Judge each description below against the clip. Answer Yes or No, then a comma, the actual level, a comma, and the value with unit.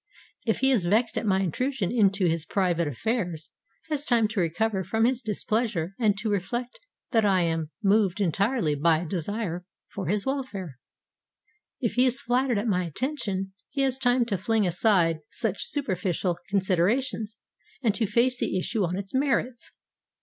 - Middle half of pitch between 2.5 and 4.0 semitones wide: No, average, 4.9 semitones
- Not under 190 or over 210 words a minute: No, average, 170 wpm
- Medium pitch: No, high, 205 Hz